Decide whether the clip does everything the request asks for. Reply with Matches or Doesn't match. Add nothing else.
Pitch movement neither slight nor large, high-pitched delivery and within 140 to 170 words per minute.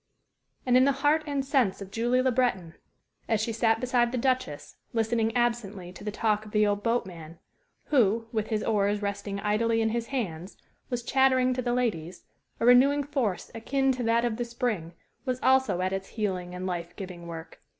Doesn't match